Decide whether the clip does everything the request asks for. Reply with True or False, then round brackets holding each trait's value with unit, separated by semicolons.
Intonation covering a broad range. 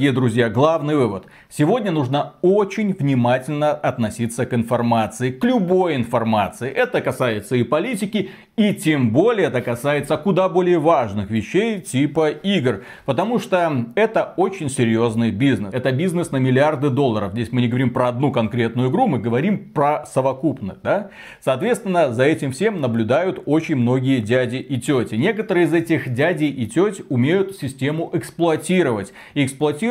True (5.8 semitones)